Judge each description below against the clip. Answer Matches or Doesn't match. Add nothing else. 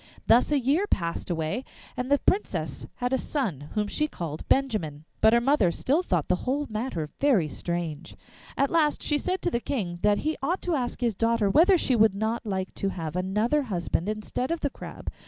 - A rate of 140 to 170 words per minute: Doesn't match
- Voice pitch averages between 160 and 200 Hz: Doesn't match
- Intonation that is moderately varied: Doesn't match